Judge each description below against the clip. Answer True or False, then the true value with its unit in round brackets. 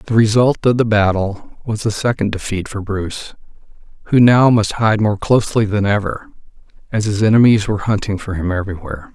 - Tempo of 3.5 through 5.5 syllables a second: False (5.7 syllables/s)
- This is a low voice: True (105 Hz)